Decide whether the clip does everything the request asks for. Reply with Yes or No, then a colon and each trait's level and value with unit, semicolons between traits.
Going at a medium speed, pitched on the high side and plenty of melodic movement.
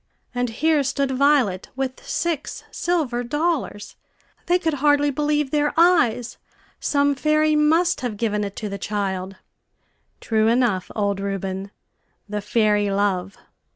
No: slow, 130 wpm; high, 245 Hz; wide, 6.4 semitones